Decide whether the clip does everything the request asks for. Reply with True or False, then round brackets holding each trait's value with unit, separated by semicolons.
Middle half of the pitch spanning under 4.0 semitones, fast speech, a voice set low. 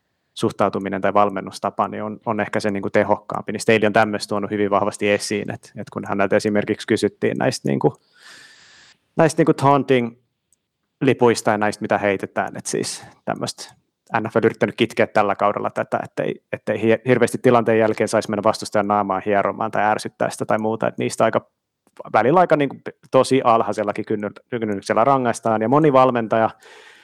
True (2.4 semitones; 175 wpm; 110 Hz)